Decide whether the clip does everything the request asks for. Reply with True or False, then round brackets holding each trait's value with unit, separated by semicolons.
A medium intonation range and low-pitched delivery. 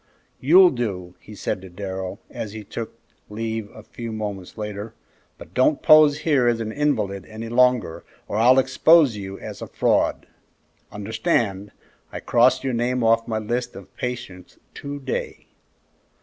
True (3.6 semitones; 115 Hz)